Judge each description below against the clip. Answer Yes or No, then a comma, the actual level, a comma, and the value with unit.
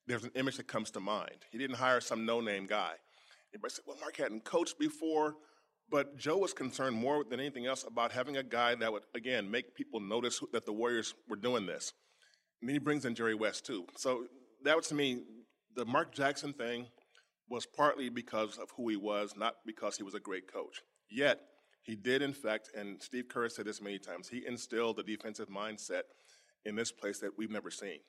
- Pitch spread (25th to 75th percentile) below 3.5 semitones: No, average, 4.2 semitones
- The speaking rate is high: Yes, fast, 210 wpm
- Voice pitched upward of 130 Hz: No, low, 120 Hz